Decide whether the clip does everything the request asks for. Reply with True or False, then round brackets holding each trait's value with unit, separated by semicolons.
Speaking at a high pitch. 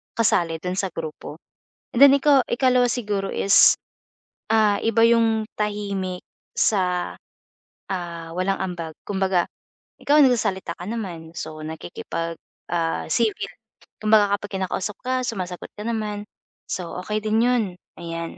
True (200 Hz)